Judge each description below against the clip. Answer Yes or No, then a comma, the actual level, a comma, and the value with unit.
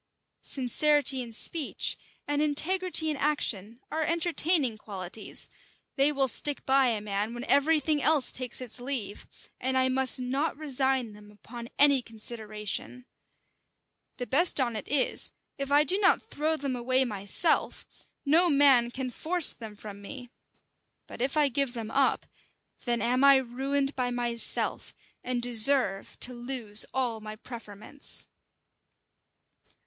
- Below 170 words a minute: Yes, average, 145 wpm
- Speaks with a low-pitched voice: No, very high, 260 Hz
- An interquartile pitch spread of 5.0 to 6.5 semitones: No, average, 3.4 semitones